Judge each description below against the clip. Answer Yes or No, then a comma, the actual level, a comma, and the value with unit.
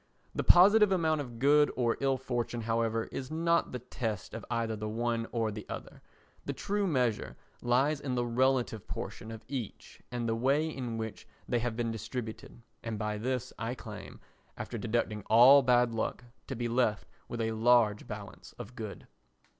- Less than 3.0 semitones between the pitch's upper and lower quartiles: Yes, narrow, 2.6 semitones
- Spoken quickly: No, average, 180 wpm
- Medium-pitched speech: No, low, 120 Hz